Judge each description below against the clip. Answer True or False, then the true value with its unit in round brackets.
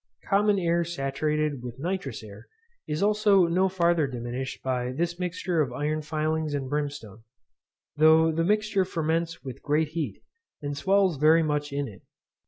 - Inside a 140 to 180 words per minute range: True (155 wpm)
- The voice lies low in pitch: False (155 Hz)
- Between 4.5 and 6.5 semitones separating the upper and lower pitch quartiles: False (3.5 semitones)